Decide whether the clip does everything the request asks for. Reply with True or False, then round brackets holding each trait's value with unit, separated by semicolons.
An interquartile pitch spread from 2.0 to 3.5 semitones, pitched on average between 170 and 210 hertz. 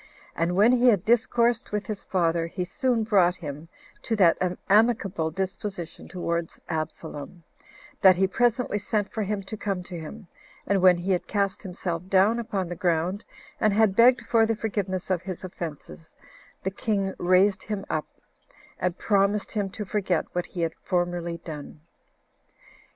True (3.2 semitones; 190 Hz)